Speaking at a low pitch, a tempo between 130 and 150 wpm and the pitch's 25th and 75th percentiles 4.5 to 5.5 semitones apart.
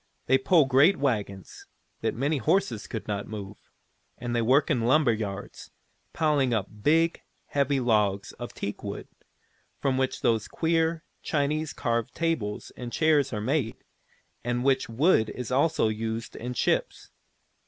Yes: low, 125 Hz; average, 145 wpm; average, 5.0 semitones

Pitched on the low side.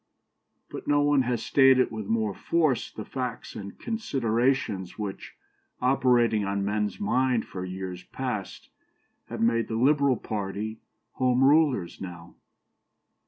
Yes: low, 115 Hz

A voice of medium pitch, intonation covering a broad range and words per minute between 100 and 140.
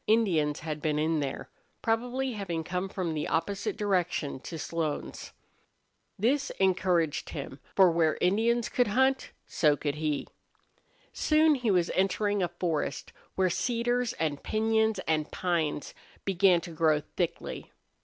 Yes: medium, 180 Hz; wide, 5.7 semitones; slow, 135 wpm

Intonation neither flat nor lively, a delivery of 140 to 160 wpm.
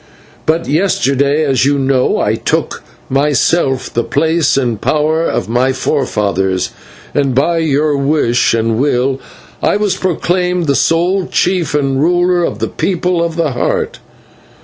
Yes: average, 4.2 semitones; average, 150 wpm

